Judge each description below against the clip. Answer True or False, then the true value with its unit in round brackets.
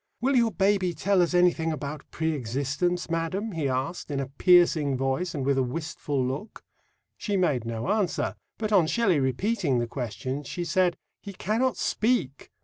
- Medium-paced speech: True (170 wpm)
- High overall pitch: False (165 Hz)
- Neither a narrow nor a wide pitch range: False (6.0 semitones)